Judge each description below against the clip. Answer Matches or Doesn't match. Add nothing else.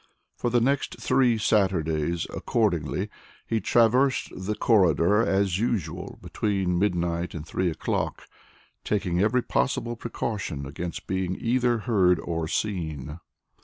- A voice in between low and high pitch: Doesn't match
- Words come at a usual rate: Doesn't match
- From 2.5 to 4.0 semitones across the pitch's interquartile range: Doesn't match